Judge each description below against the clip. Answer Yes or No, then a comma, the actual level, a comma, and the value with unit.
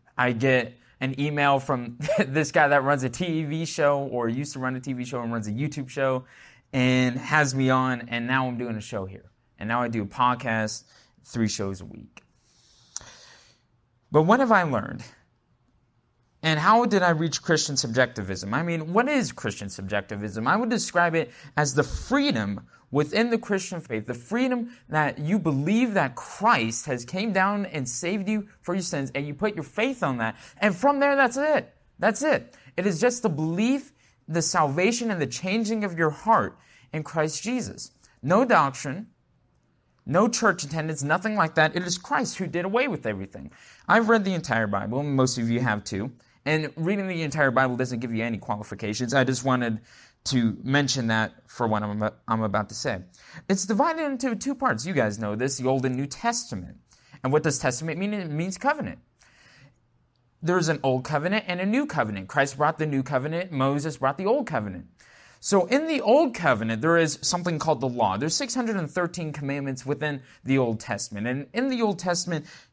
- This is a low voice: No, medium, 145 Hz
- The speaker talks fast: No, average, 190 wpm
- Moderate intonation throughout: No, wide, 7.1 semitones